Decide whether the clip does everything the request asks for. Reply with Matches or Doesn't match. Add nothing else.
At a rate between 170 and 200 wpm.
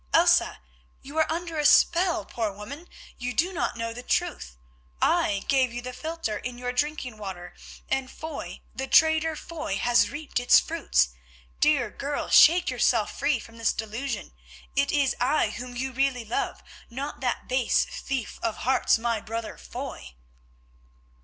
Doesn't match